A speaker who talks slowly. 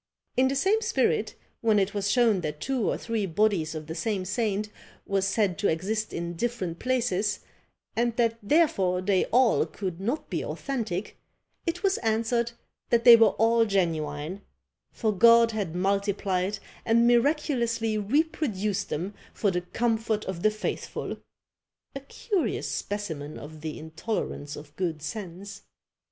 No: average, 145 wpm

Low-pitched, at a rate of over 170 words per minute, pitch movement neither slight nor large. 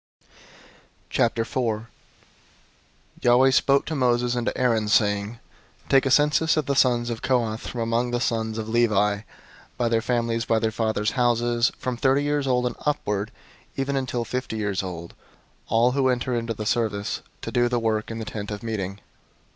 No: low, 120 Hz; average, 180 wpm; narrow, 2.3 semitones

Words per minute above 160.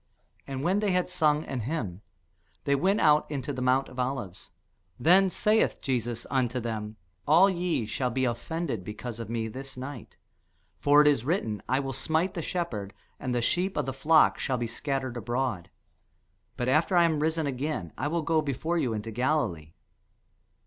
Yes: average, 180 wpm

